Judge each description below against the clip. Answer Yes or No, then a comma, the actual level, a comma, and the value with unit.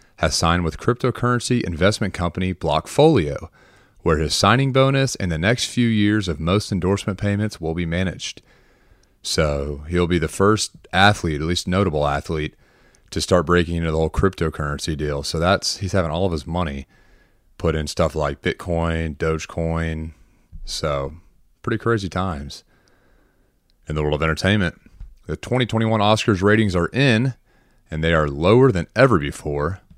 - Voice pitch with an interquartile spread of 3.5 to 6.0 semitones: Yes, average, 4.5 semitones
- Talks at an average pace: Yes, average, 155 wpm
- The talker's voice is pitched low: Yes, very low, 90 Hz